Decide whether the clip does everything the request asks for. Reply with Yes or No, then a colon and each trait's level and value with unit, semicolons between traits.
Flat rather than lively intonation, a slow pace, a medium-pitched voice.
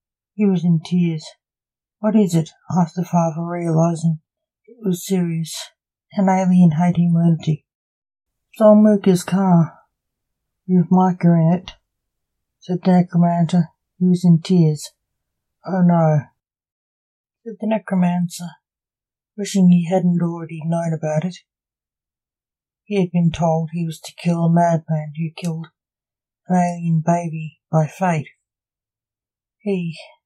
Yes: narrow, 2.3 semitones; slow, 120 wpm; medium, 170 Hz